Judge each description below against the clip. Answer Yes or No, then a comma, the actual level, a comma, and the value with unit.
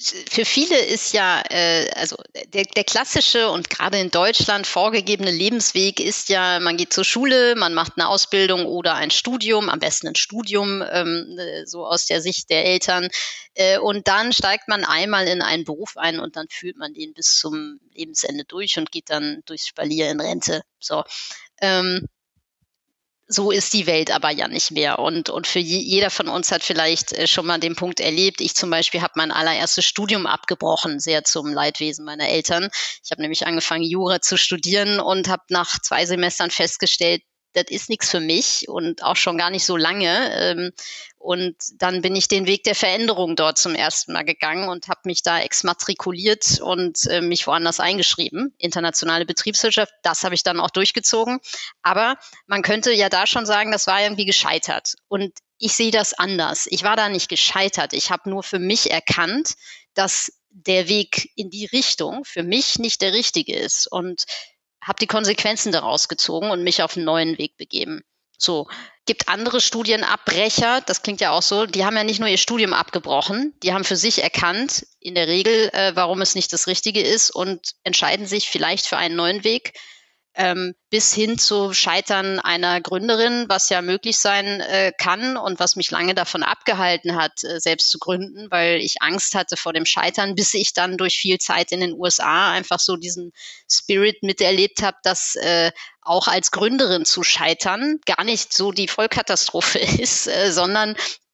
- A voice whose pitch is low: No, medium, 185 Hz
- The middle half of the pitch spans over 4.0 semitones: No, average, 3.3 semitones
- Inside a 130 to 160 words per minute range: No, average, 180 wpm